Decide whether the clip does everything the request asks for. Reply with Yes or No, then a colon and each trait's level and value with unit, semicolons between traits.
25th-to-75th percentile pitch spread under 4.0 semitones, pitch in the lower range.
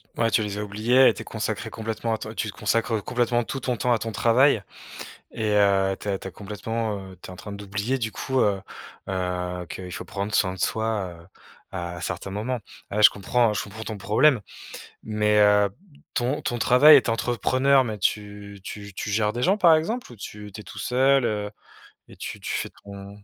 Yes: average, 3.1 semitones; low, 105 Hz